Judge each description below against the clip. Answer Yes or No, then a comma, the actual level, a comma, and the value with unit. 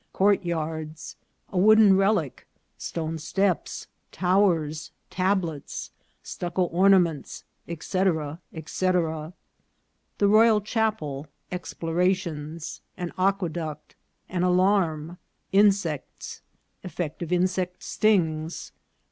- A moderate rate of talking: No, slow, 105 wpm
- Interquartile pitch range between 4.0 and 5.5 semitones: No, average, 3.4 semitones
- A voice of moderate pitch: Yes, medium, 180 Hz